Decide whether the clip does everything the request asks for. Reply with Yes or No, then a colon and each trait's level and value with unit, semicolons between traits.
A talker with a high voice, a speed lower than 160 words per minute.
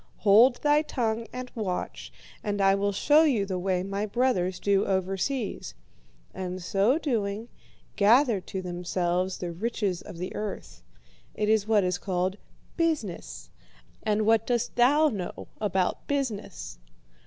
Yes: high, 205 Hz; average, 140 wpm